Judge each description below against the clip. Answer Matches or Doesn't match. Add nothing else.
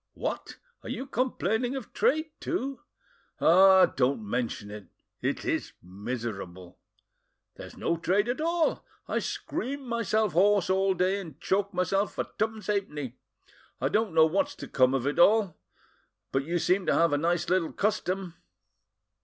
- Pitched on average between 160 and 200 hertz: Matches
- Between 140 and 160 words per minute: Matches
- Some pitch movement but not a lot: Doesn't match